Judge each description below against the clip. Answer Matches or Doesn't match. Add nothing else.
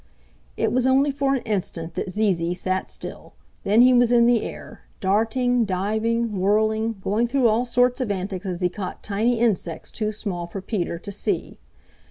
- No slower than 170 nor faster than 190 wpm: Matches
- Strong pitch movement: Doesn't match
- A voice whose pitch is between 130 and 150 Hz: Doesn't match